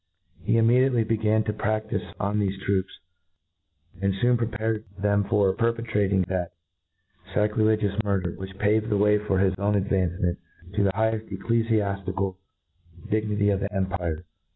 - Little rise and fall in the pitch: Yes, narrow, 2.1 semitones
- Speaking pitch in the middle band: No, low, 105 Hz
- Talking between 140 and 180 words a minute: Yes, average, 145 wpm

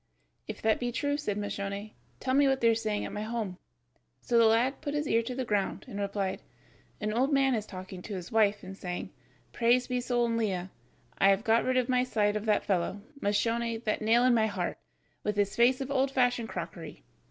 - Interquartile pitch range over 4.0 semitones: No, average, 3.5 semitones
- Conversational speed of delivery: No, fast, 220 wpm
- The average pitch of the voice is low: No, high, 225 Hz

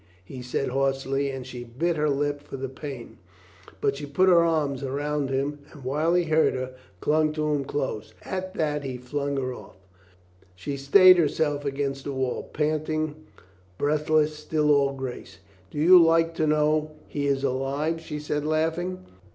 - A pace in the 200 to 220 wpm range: No, average, 170 wpm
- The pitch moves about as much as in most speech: No, narrow, 2.3 semitones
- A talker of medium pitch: Yes, medium, 145 Hz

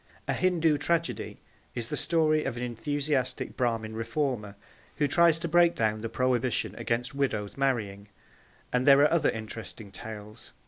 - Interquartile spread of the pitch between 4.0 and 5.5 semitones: Yes, average, 5.2 semitones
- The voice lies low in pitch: Yes, low, 125 Hz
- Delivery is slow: No, average, 150 wpm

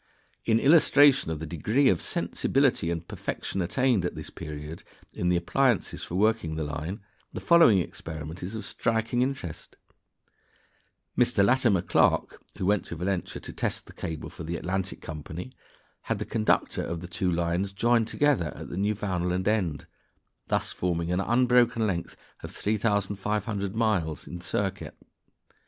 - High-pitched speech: No, very low, 95 Hz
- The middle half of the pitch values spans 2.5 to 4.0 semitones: No, average, 4.8 semitones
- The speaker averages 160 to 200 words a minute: No, average, 150 wpm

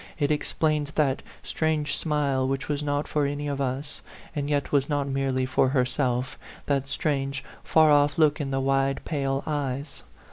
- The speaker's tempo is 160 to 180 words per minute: Yes, average, 170 wpm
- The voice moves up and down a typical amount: No, narrow, 1.5 semitones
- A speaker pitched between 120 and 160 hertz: Yes, medium, 140 Hz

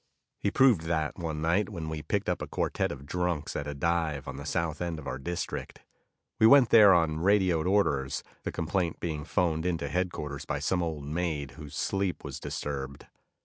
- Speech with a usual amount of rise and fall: Yes, average, 3.4 semitones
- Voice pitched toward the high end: No, very low, 80 Hz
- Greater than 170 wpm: Yes, average, 190 wpm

